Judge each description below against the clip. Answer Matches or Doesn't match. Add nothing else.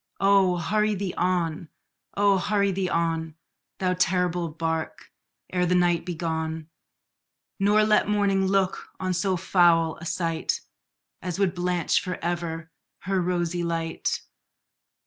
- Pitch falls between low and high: Matches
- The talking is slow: Matches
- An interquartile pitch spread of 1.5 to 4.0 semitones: Matches